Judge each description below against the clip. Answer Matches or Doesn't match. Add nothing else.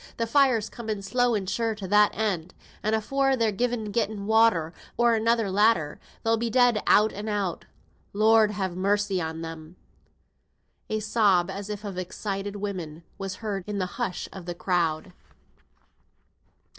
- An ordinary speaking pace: Matches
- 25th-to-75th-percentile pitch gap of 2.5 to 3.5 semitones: Matches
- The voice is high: Matches